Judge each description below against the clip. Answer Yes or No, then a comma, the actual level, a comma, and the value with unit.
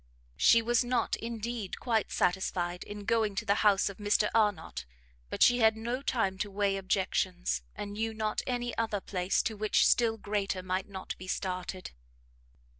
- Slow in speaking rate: No, average, 170 wpm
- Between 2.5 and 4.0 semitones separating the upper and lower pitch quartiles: Yes, average, 2.9 semitones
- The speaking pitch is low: No, high, 205 Hz